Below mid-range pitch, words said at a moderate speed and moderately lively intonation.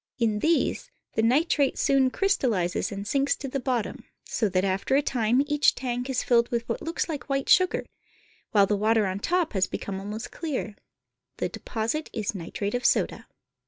No: high, 240 Hz; average, 180 wpm; average, 4.9 semitones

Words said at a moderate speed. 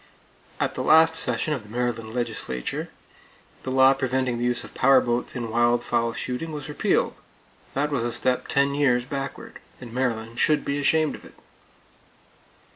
Yes: average, 170 wpm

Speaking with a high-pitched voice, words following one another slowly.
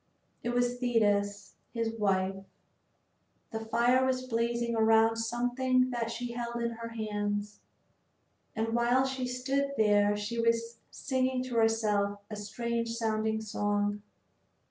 Yes: high, 230 Hz; slow, 125 wpm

